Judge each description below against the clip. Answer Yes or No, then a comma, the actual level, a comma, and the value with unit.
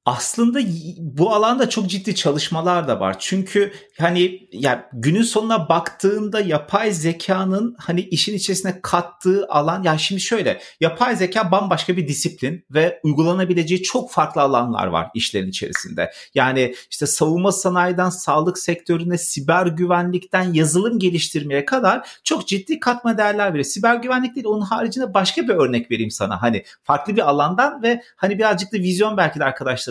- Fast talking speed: Yes, fast, 155 wpm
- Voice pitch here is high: No, medium, 180 Hz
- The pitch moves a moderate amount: Yes, average, 4.7 semitones